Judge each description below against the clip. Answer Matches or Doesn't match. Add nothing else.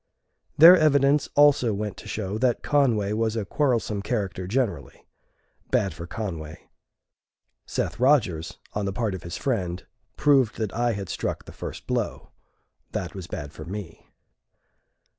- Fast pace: Doesn't match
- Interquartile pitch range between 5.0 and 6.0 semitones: Matches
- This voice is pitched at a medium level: Doesn't match